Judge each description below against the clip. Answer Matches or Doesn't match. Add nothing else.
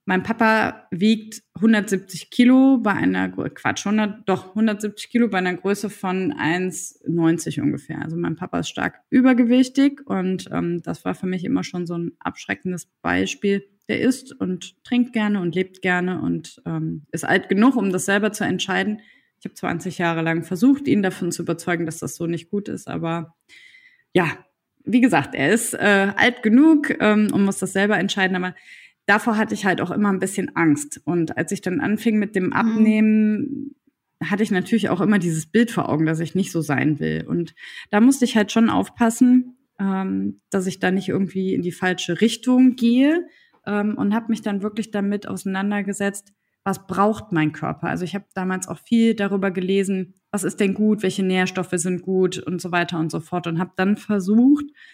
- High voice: Matches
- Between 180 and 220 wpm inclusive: Matches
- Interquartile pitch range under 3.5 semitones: Doesn't match